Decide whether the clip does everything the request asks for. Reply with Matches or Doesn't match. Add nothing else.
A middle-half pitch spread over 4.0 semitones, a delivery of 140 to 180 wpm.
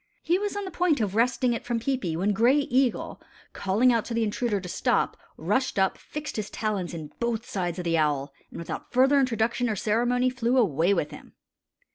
Doesn't match